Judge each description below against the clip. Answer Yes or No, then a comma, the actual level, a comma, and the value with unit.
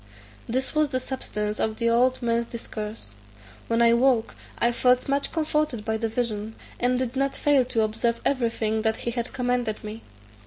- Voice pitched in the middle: No, high, 235 Hz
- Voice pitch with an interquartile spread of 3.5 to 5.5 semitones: No, narrow, 2.6 semitones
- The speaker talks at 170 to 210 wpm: Yes, average, 180 wpm